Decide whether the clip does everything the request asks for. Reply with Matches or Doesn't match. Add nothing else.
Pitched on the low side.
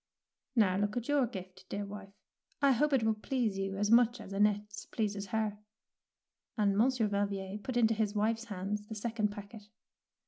Doesn't match